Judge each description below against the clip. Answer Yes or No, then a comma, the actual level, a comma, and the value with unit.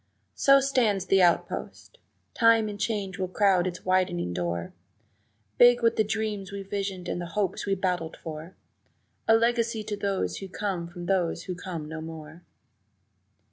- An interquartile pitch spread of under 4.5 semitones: Yes, average, 3.4 semitones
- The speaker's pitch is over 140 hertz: Yes, high, 190 Hz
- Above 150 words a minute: Yes, average, 160 wpm